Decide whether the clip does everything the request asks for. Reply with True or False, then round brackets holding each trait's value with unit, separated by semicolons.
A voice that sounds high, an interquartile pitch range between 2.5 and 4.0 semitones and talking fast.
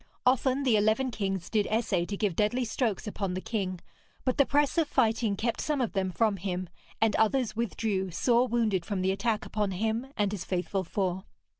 False (215 Hz; 3.7 semitones; 195 wpm)